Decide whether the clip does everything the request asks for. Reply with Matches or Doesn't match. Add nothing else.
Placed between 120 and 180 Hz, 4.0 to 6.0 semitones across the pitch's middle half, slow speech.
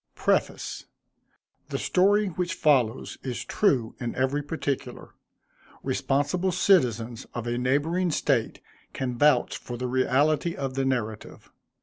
Matches